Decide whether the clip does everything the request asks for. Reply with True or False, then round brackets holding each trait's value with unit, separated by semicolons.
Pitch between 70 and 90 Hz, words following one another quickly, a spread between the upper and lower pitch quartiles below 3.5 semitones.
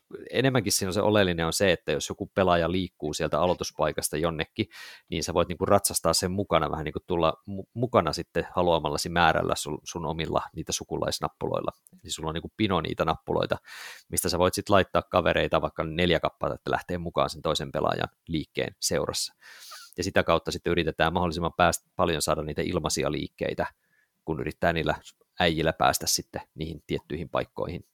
True (85 Hz; 175 wpm; 3.0 semitones)